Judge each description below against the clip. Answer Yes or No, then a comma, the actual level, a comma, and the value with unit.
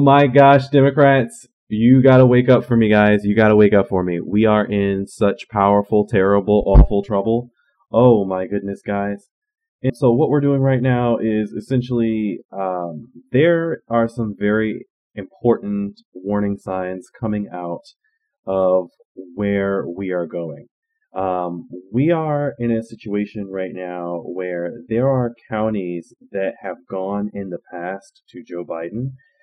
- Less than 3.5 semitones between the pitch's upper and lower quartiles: No, average, 4.5 semitones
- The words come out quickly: No, average, 155 wpm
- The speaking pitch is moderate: No, low, 105 Hz